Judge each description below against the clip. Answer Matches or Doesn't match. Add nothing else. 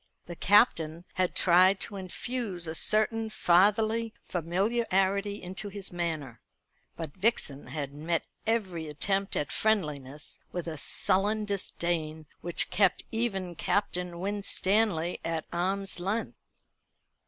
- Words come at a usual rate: Doesn't match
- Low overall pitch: Doesn't match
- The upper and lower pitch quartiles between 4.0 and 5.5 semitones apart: Doesn't match